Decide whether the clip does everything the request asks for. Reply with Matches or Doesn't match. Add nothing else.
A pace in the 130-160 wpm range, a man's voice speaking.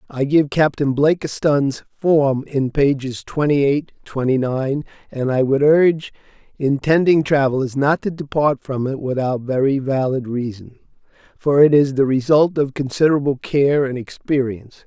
Matches